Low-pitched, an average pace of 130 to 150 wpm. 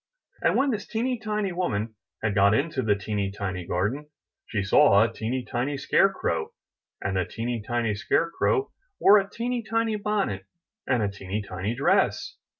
No: low, 120 Hz; average, 170 wpm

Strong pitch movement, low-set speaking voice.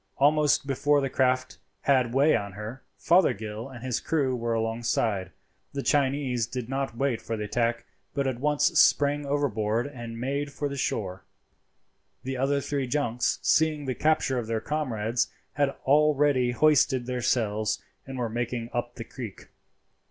No: average, 3.5 semitones; low, 130 Hz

